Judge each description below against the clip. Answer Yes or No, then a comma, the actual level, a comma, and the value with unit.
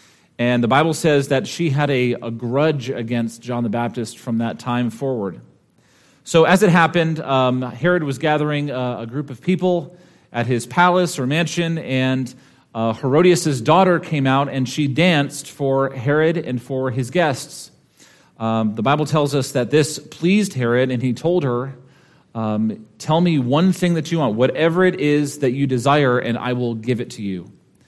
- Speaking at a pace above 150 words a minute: Yes, average, 185 wpm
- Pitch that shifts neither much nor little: Yes, average, 4.5 semitones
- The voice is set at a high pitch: No, low, 135 Hz